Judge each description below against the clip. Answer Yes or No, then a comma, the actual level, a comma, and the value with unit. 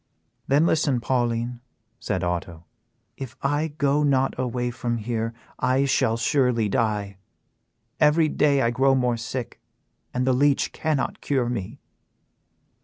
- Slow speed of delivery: Yes, slow, 130 wpm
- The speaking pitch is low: Yes, low, 125 Hz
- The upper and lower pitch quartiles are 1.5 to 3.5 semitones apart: Yes, average, 3.1 semitones